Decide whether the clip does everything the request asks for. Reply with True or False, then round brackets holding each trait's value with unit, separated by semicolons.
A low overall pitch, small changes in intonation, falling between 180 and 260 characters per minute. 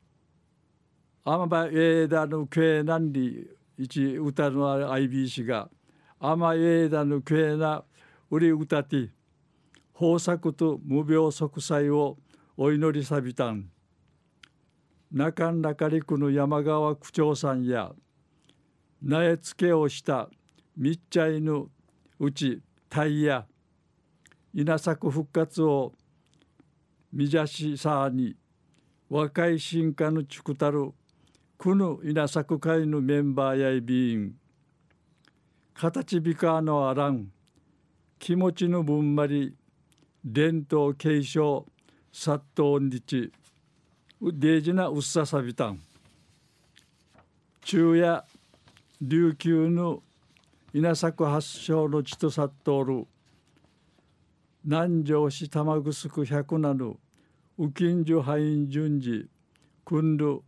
False (150 Hz; 2.2 semitones; 185 characters per minute)